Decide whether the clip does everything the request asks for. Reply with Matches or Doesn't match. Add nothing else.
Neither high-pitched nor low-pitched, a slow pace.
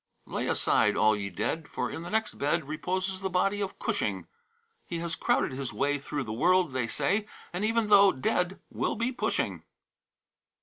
Doesn't match